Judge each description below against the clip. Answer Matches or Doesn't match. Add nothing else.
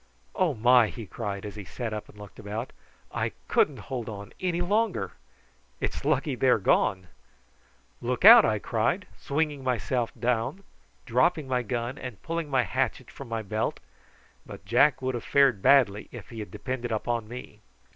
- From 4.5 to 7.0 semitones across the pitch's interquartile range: Doesn't match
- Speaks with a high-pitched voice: Doesn't match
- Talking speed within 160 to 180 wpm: Matches